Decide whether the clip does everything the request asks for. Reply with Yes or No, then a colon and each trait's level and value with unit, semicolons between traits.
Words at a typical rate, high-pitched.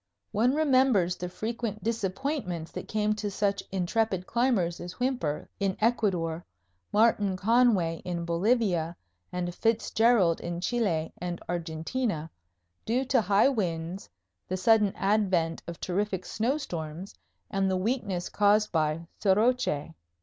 No: slow, 120 wpm; high, 195 Hz